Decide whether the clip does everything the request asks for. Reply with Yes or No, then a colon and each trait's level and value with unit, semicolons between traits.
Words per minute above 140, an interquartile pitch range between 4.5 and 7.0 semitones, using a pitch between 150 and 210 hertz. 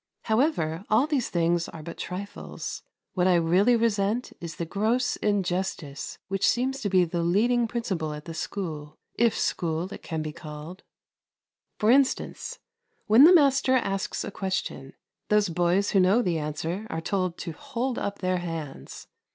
Yes: average, 160 wpm; average, 5.2 semitones; high, 190 Hz